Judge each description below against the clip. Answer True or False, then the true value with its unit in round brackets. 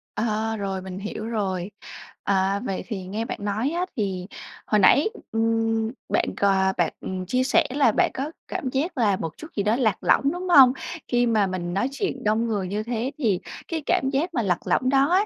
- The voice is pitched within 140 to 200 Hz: False (225 Hz)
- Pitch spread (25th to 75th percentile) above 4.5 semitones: True (5.1 semitones)